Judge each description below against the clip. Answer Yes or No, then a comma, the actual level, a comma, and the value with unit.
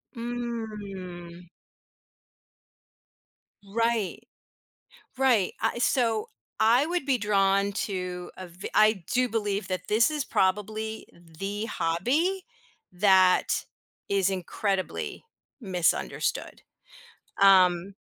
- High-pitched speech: Yes, high, 200 Hz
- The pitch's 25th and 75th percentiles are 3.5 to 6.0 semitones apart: Yes, average, 3.8 semitones